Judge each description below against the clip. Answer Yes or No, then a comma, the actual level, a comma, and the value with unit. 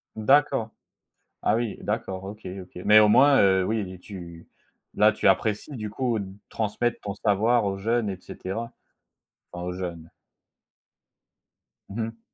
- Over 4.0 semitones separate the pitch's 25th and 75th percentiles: No, average, 3.0 semitones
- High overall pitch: No, low, 105 Hz